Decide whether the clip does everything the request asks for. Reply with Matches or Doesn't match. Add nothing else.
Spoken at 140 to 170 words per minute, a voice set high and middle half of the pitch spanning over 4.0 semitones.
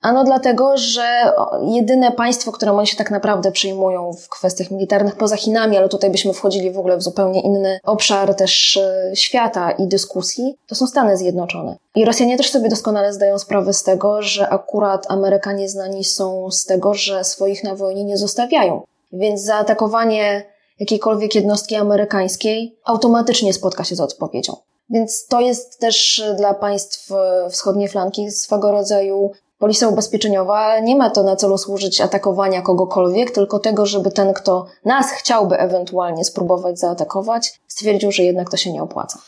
Doesn't match